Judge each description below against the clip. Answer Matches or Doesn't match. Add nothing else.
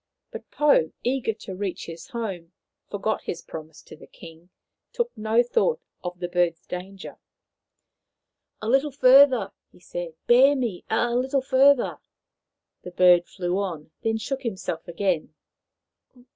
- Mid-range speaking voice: Doesn't match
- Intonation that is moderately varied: Doesn't match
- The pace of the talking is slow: Doesn't match